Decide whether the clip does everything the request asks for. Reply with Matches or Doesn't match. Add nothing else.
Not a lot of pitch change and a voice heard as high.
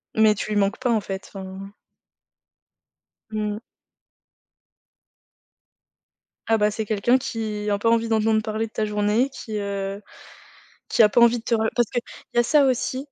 Matches